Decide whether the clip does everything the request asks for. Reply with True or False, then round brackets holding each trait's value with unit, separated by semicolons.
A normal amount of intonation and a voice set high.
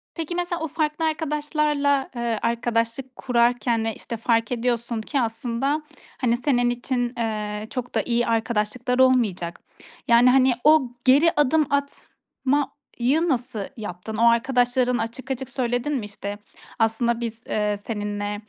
True (3.0 semitones; 245 Hz)